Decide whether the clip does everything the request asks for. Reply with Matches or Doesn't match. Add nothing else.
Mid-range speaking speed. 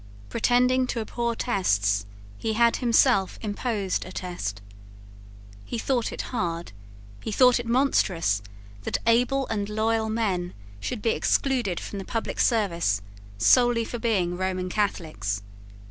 Doesn't match